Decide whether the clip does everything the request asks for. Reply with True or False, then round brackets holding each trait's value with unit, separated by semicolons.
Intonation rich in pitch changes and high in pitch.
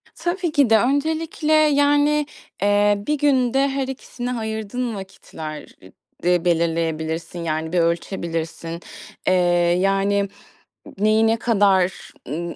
True (8.2 semitones; 205 Hz)